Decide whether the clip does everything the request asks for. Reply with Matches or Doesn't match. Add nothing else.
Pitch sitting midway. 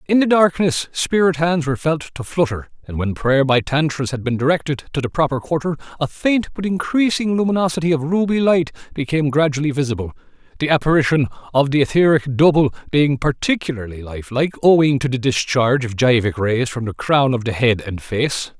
Matches